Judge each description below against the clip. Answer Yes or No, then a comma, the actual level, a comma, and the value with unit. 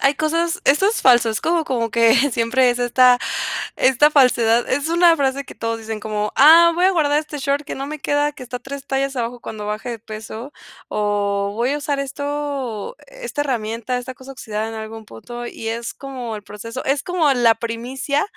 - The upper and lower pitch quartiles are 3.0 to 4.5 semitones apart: Yes, average, 4.1 semitones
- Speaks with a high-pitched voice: Yes, very high, 255 Hz